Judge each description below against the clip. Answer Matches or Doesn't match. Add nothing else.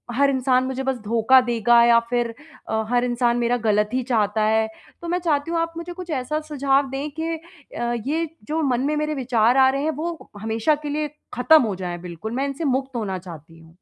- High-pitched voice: Matches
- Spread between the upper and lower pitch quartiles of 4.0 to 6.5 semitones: Matches